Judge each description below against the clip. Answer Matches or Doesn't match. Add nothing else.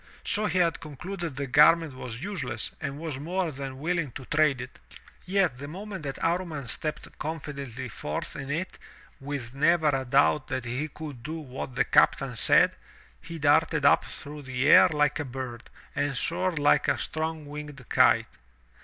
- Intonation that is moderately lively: Matches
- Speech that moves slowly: Doesn't match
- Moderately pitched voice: Matches